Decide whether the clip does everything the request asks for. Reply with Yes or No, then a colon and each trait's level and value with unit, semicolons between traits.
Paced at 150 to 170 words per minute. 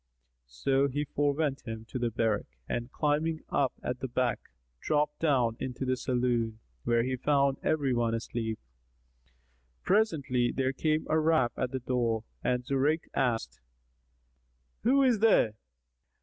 No: average, 140 wpm